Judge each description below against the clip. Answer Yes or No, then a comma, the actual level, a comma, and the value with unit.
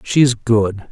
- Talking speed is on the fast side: No, average, 195 wpm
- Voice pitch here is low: Yes, low, 115 Hz